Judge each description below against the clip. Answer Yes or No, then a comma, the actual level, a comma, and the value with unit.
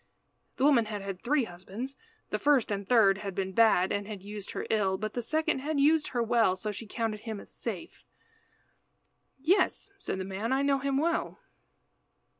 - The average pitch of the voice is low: No, high, 225 Hz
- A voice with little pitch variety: No, wide, 5.5 semitones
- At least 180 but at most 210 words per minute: Yes, average, 190 wpm